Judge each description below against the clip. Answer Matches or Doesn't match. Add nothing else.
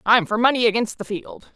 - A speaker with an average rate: Doesn't match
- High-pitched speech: Matches